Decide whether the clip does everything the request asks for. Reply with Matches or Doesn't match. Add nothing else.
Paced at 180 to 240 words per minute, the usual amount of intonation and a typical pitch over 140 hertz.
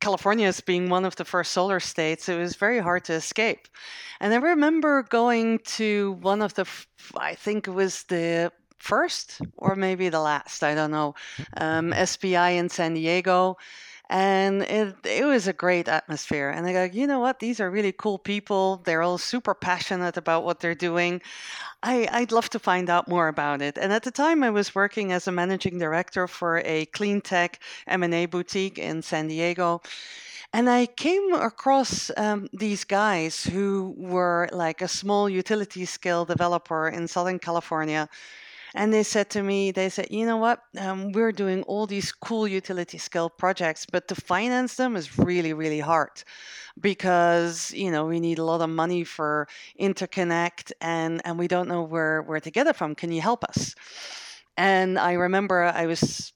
Matches